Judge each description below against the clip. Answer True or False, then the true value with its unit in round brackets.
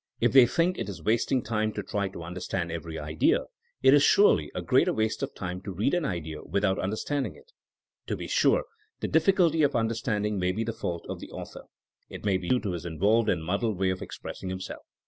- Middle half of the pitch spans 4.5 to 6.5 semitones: True (4.9 semitones)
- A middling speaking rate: False (225 wpm)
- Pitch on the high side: False (105 Hz)